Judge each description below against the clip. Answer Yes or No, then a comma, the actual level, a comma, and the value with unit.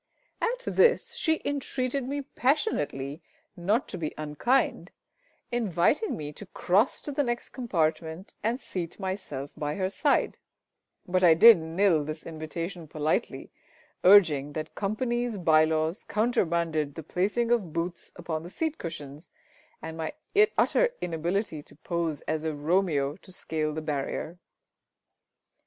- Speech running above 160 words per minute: No, slow, 135 wpm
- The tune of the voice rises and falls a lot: Yes, wide, 6.4 semitones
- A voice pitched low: No, medium, 170 Hz